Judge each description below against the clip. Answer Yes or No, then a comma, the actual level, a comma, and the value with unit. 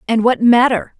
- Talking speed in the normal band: Yes, average, 180 wpm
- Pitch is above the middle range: Yes, high, 235 Hz